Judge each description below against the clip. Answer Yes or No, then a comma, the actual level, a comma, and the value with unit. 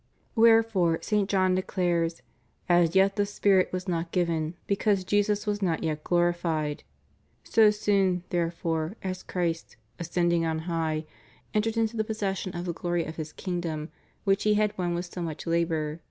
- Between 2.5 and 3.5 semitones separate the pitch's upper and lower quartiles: Yes, average, 3.2 semitones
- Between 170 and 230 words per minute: No, average, 155 wpm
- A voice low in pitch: No, medium, 175 Hz